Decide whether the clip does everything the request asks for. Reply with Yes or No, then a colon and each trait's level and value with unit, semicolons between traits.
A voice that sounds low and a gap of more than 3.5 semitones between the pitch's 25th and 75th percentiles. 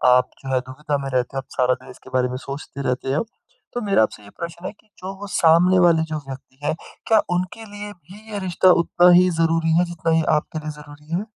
No: medium, 160 Hz; average, 5.2 semitones